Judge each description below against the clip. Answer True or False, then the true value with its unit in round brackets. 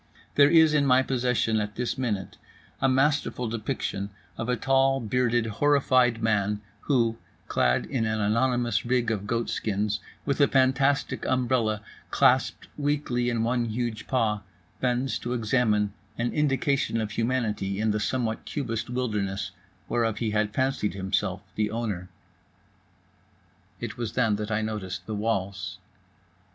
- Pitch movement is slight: False (3.4 semitones)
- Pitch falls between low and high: False (115 Hz)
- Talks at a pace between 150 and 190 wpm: False (140 wpm)